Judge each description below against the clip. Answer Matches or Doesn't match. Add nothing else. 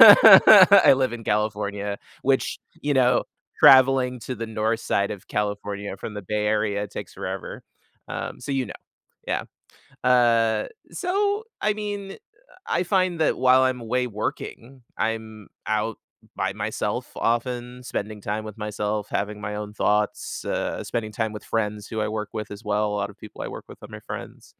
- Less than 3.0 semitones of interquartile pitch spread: Doesn't match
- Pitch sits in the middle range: Doesn't match